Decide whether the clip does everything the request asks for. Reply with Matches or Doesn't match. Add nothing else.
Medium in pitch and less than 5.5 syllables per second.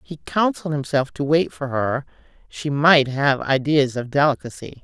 Matches